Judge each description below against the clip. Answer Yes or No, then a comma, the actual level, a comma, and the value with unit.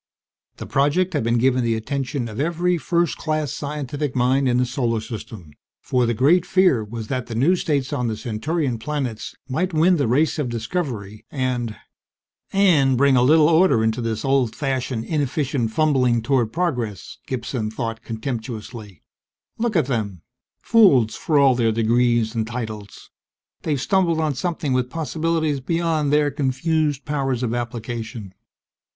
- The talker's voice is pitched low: Yes, low, 130 Hz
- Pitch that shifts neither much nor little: Yes, average, 4.7 semitones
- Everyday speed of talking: Yes, average, 155 wpm